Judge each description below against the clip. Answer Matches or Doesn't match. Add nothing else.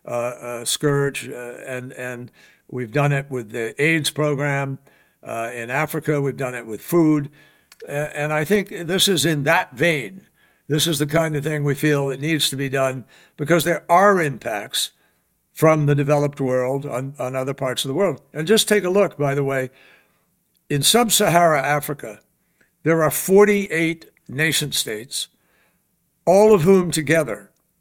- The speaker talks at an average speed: Matches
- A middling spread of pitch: Matches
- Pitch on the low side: Doesn't match